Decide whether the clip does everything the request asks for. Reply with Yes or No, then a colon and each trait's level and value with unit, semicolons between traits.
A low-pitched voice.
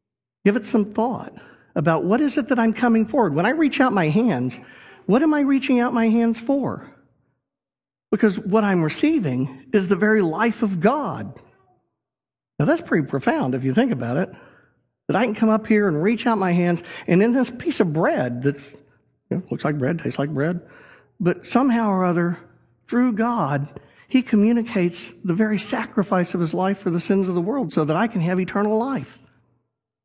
No: high, 210 Hz